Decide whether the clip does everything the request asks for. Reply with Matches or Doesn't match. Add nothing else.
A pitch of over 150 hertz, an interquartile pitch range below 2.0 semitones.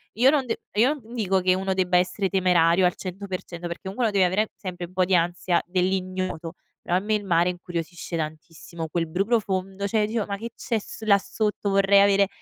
Doesn't match